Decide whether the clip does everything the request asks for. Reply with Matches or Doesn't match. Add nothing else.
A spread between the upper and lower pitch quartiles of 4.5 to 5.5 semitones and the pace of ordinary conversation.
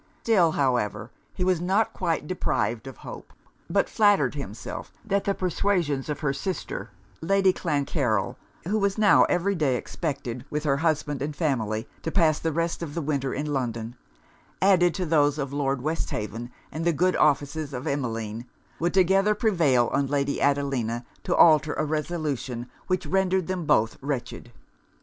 Matches